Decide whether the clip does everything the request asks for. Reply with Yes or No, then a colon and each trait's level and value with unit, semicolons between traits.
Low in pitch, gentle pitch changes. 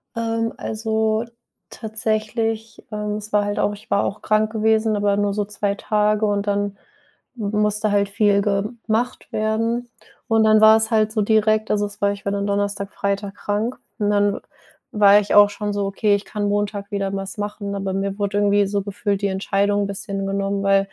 No: high, 205 Hz; narrow, 1.3 semitones